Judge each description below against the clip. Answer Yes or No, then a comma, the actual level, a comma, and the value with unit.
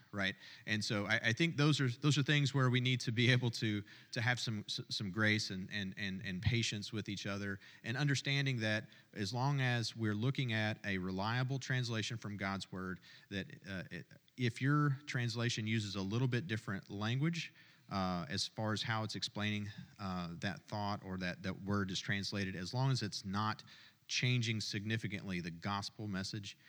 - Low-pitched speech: Yes, low, 110 Hz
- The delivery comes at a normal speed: Yes, average, 185 wpm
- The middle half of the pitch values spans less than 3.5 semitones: No, average, 4.0 semitones